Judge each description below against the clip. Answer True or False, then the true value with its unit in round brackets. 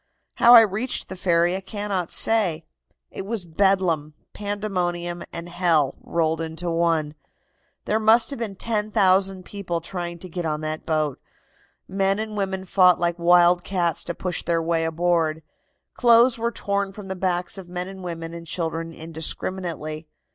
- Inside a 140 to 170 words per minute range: True (160 wpm)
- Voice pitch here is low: False (175 Hz)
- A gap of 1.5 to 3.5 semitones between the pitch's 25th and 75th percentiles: True (2.9 semitones)